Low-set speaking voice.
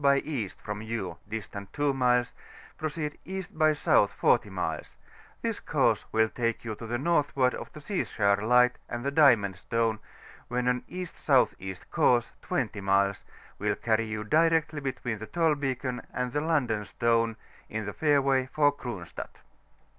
Yes: low, 125 Hz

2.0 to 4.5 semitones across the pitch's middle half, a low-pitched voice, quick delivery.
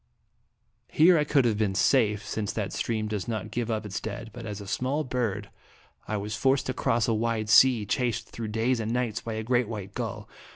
Yes: average, 2.7 semitones; low, 110 Hz; fast, 215 wpm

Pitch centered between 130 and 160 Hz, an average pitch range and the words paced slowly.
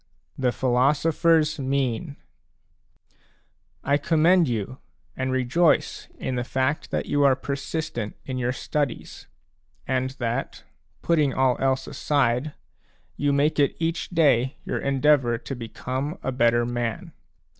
Yes: low, 135 Hz; average, 3.0 semitones; slow, 125 wpm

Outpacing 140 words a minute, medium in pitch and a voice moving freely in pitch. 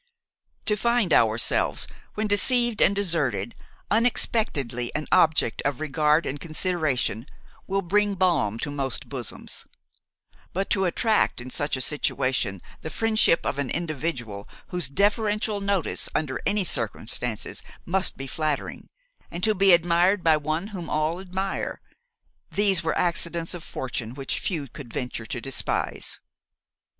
No: slow, 135 wpm; medium, 165 Hz; wide, 6.5 semitones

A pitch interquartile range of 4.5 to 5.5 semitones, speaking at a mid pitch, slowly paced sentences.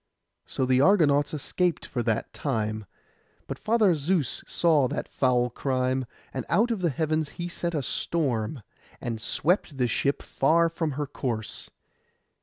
No: average, 4.8 semitones; medium, 145 Hz; average, 150 wpm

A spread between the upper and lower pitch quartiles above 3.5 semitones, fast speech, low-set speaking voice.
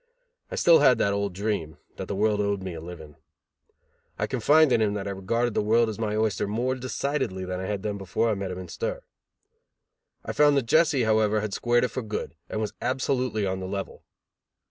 Yes: average, 4.2 semitones; fast, 215 wpm; low, 110 Hz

